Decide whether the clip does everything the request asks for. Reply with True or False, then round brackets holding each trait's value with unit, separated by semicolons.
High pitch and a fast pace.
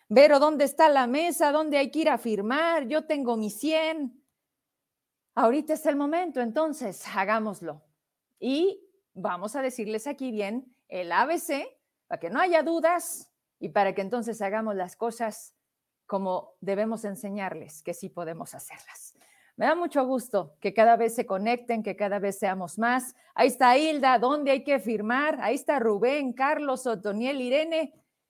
False (245 Hz; 160 wpm)